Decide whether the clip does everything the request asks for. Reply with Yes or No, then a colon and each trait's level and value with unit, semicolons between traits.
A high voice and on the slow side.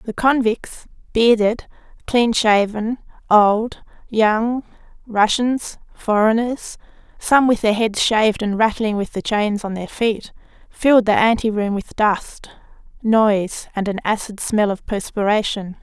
Yes: high, 220 Hz; slow, 130 wpm